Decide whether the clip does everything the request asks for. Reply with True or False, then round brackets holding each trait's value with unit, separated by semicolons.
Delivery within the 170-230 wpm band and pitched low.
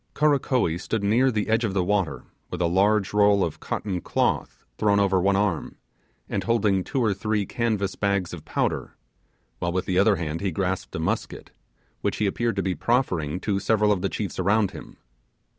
True (190 wpm; 100 Hz)